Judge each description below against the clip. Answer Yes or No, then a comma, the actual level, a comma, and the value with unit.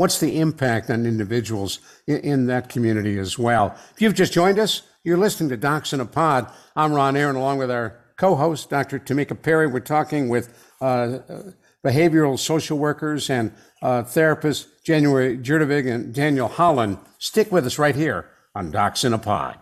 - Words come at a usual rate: Yes, average, 175 wpm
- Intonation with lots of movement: No, average, 4.2 semitones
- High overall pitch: No, medium, 140 Hz